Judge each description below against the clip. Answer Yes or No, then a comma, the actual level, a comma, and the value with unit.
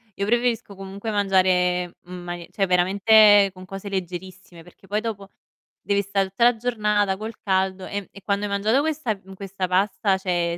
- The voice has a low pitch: No, high, 195 Hz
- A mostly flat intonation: Yes, narrow, 1.9 semitones